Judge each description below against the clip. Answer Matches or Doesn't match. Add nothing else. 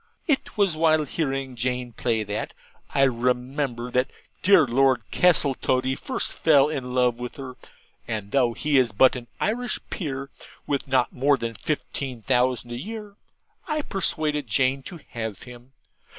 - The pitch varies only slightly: Doesn't match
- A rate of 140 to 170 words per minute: Matches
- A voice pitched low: Matches